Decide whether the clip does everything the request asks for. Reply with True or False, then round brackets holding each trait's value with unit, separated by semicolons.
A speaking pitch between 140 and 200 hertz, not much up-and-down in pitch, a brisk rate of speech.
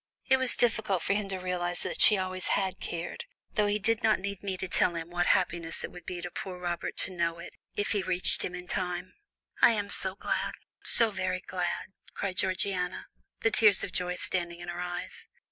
True (185 Hz; 2.2 semitones; 215 wpm)